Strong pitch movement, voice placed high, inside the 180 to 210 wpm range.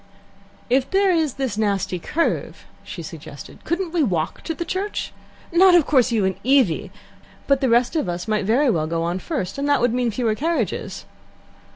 Yes: wide, 7.6 semitones; very high, 255 Hz; average, 190 wpm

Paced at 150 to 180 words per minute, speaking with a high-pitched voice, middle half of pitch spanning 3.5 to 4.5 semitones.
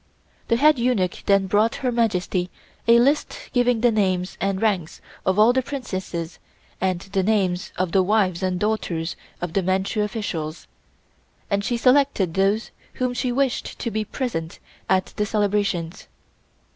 Yes: average, 155 wpm; high, 200 Hz; average, 4.1 semitones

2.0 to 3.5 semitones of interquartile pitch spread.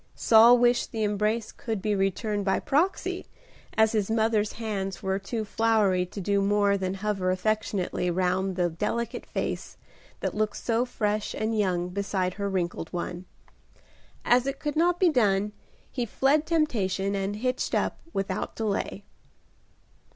Yes: average, 2.9 semitones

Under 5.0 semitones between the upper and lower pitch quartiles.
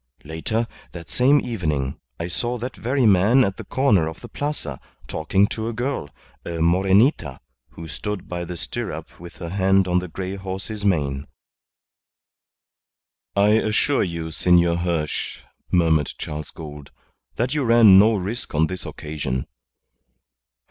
No: average, 5.3 semitones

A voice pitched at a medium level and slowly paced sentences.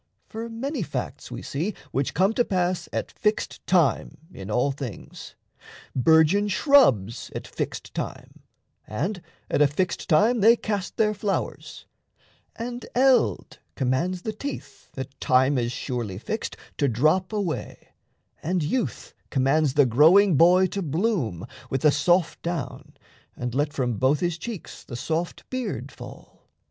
No: medium, 165 Hz; average, 145 wpm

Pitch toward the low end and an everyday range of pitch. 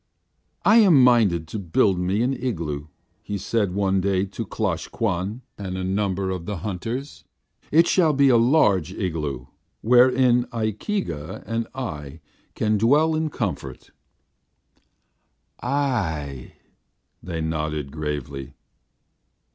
No: low, 100 Hz; wide, 7.2 semitones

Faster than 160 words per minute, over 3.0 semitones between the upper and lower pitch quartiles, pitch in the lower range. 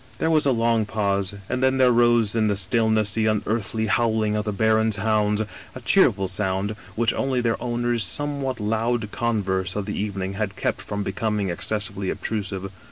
No: average, 185 wpm; narrow, 2.6 semitones; low, 110 Hz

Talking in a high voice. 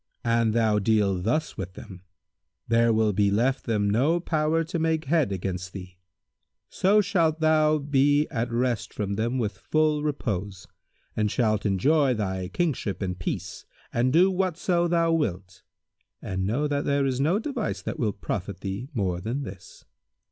No: low, 120 Hz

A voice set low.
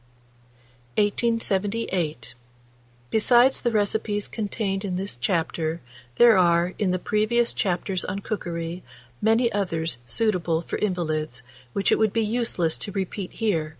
No: high, 195 Hz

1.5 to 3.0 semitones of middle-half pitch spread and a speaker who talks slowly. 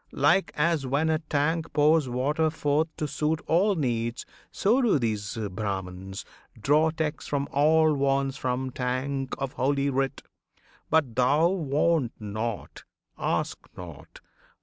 No: average, 4.1 semitones; slow, 130 wpm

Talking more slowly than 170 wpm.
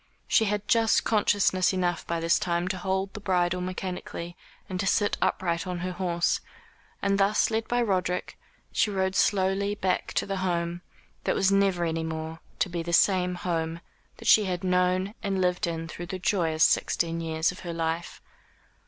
No: average, 180 wpm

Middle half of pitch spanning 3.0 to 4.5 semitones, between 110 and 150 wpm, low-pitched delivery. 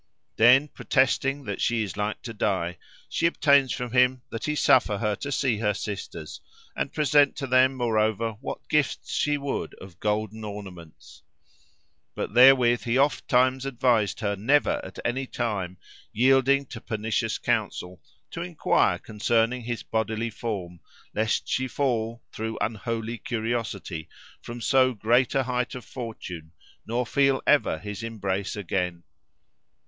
Yes: average, 3.7 semitones; average, 145 wpm; low, 115 Hz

